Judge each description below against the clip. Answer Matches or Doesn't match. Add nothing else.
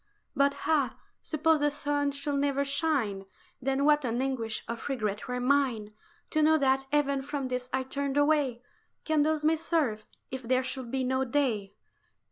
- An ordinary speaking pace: Matches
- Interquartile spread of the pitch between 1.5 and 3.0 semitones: Matches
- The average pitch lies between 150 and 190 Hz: Doesn't match